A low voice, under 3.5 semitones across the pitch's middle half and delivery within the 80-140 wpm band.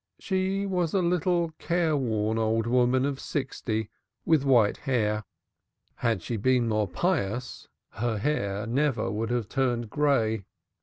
No: low, 125 Hz; average, 5.3 semitones; slow, 135 wpm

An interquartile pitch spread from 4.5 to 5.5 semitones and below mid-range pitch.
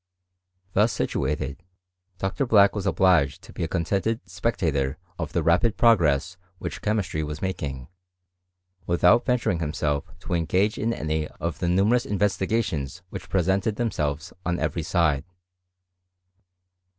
Yes: average, 5.0 semitones; very low, 90 Hz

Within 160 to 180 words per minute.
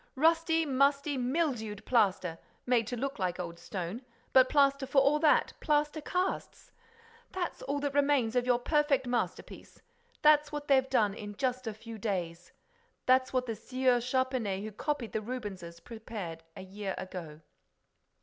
No: average, 145 wpm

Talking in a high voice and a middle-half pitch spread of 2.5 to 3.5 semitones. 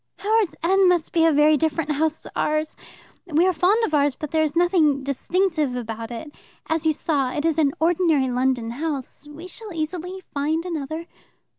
Yes: very high, 315 Hz; average, 3.2 semitones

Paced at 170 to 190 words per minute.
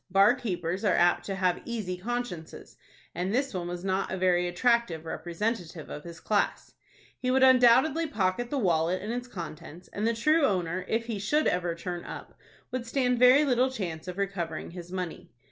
Yes: average, 185 wpm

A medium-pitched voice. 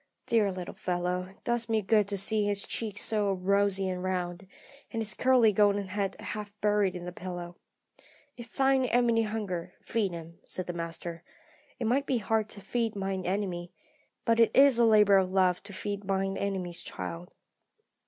No: high, 200 Hz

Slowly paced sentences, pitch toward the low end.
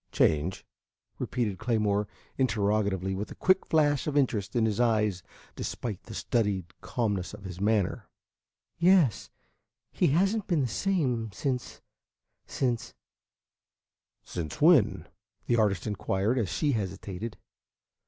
Yes: slow, 125 wpm; low, 110 Hz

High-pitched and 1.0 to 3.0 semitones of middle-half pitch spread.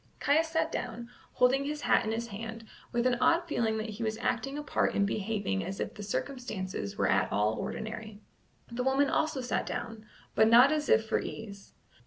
No: high, 230 Hz; average, 3.8 semitones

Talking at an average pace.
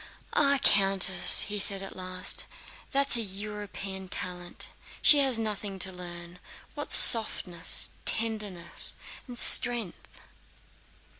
No: slow, 100 wpm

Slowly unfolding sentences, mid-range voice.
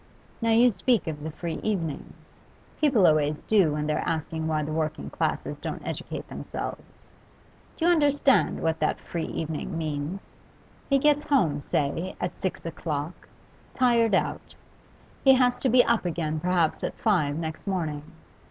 No: average, 155 wpm; medium, 170 Hz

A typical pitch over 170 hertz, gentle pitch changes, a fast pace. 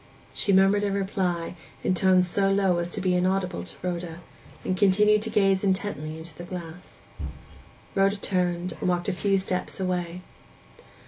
No: medium, 185 Hz; narrow, 1.9 semitones; average, 165 wpm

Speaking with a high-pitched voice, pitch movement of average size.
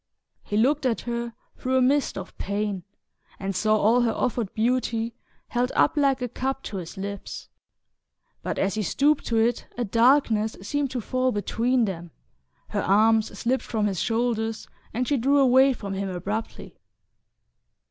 Yes: high, 230 Hz; average, 3.5 semitones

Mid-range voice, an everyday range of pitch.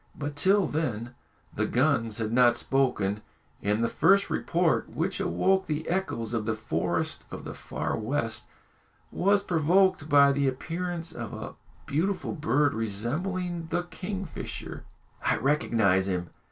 No: medium, 145 Hz; wide, 7.5 semitones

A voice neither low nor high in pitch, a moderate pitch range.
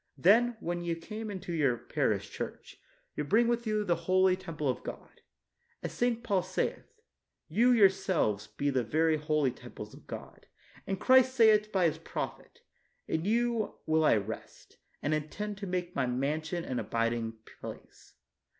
No: medium, 175 Hz; wide, 6.1 semitones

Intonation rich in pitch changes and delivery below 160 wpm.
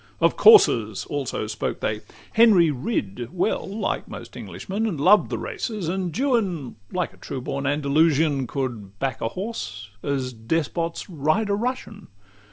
Yes: wide, 7.8 semitones; average, 150 wpm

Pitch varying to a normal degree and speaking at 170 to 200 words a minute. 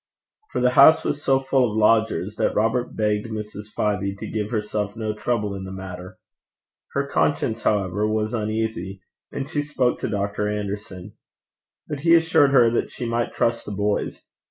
Yes: average, 3.1 semitones; average, 175 wpm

